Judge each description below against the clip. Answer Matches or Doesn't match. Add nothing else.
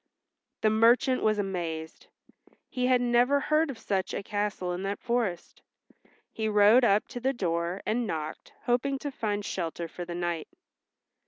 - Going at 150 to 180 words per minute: Matches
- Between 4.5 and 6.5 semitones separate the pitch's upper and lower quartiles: Matches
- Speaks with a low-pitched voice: Doesn't match